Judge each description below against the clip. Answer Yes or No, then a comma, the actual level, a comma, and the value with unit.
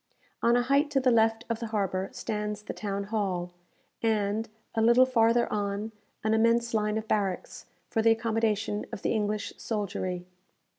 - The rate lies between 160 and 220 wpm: Yes, average, 165 wpm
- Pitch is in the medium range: No, high, 220 Hz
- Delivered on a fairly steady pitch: Yes, narrow, 2.0 semitones